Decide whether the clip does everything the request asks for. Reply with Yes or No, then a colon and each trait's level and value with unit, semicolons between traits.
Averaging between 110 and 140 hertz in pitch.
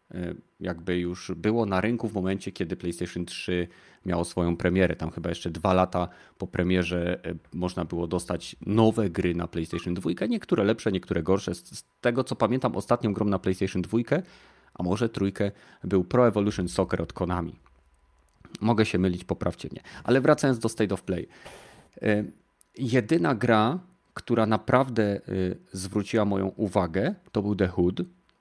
No: very low, 95 Hz